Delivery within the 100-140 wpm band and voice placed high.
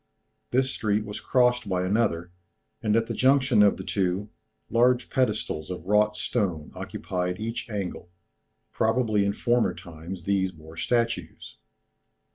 No: slow, 135 wpm; low, 105 Hz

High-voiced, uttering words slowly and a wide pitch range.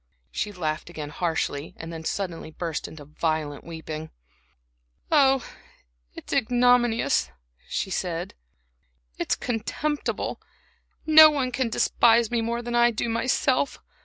Yes: high, 220 Hz; slow, 120 wpm; wide, 7.2 semitones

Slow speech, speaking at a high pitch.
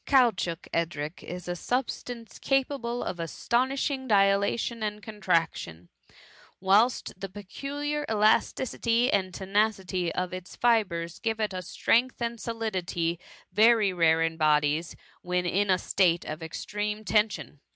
Yes: slow, 130 wpm; high, 200 Hz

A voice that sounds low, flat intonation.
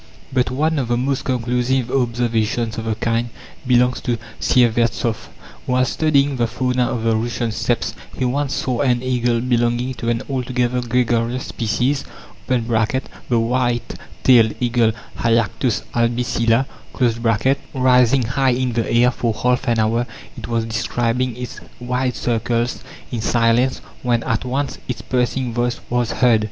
Yes: low, 120 Hz; narrow, 1.6 semitones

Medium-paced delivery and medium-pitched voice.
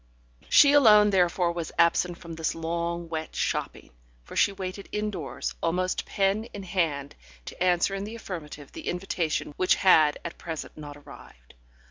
Yes: average, 155 wpm; medium, 175 Hz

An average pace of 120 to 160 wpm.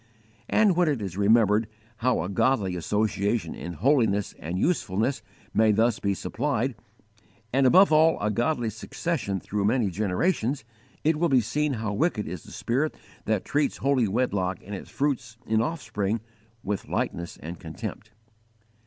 Yes: average, 155 wpm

